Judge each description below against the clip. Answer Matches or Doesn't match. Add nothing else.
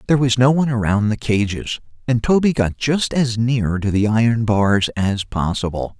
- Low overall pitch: Matches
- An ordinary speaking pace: Matches